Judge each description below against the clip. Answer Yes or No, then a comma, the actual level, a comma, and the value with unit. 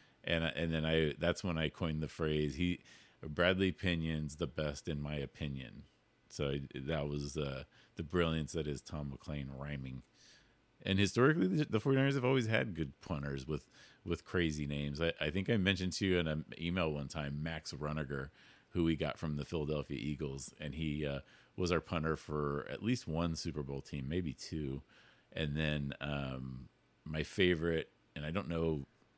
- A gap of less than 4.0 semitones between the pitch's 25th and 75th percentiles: Yes, average, 3.0 semitones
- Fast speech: No, average, 180 wpm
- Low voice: Yes, very low, 80 Hz